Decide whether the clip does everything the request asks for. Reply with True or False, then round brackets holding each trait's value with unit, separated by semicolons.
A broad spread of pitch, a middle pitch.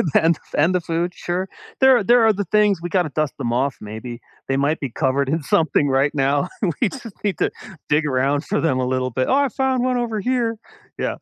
True (7.6 semitones; 165 Hz)